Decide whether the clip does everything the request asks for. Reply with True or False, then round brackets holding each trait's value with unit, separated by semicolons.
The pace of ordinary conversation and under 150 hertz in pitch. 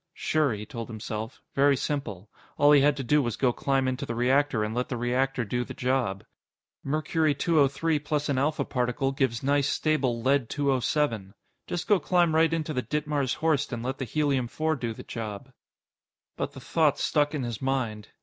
True (190 wpm; 135 Hz)